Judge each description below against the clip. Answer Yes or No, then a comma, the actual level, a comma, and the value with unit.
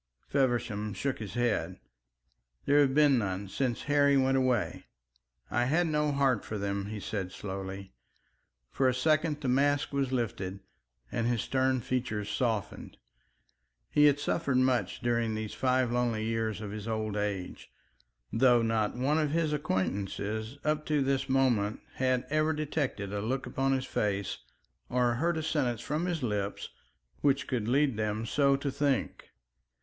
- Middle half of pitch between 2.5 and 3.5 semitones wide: No, average, 4.6 semitones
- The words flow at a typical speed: Yes, average, 155 wpm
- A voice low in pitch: Yes, low, 125 Hz